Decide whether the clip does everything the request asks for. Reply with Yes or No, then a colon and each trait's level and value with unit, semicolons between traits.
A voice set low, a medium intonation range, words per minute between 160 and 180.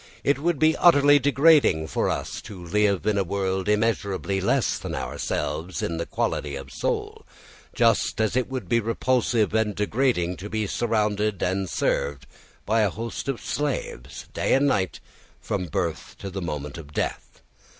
Yes: low, 105 Hz; average, 4.9 semitones; average, 165 wpm